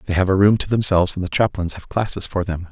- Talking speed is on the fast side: Yes, fast, 285 wpm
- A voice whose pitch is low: Yes, very low, 95 Hz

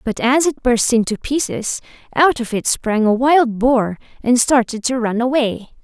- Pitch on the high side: Yes, high, 245 Hz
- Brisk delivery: No, average, 185 wpm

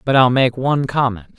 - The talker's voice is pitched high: No, low, 125 Hz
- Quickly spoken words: Yes, fast, 215 wpm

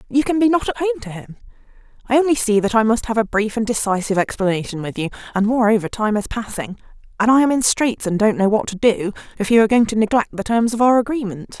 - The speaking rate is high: Yes, fast, 255 wpm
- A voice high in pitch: Yes, high, 225 Hz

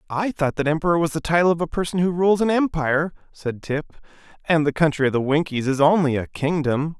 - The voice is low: No, medium, 160 Hz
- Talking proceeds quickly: Yes, fast, 225 wpm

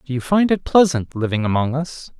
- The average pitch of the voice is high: No, medium, 145 Hz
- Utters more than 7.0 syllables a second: No, 5.4 syllables/s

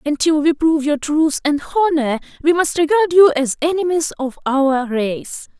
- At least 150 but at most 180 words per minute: Yes, average, 170 wpm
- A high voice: Yes, very high, 300 Hz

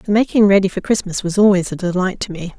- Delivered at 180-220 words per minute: No, fast, 255 wpm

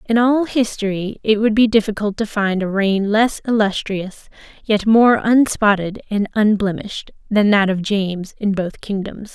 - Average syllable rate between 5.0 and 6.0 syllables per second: No, 4.5 syllables/s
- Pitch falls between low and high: No, high, 210 Hz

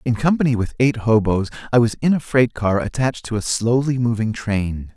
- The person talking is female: No, male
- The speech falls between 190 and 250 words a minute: Yes, fast, 205 wpm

